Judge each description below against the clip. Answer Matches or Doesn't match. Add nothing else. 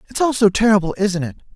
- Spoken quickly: Matches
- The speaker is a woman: Doesn't match